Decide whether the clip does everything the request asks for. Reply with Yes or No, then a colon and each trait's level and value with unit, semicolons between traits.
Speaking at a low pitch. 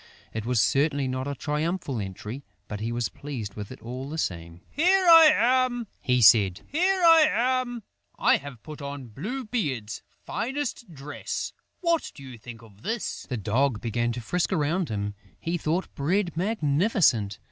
No: medium, 145 Hz